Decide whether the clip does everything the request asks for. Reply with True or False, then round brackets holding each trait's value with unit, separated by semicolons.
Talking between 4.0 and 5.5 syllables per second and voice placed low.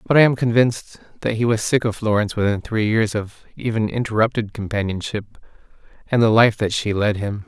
False (5.7 syllables/s; 110 Hz)